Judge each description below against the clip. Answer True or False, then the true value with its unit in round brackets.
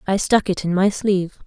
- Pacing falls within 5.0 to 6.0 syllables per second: True (5.6 syllables/s)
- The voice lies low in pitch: False (195 Hz)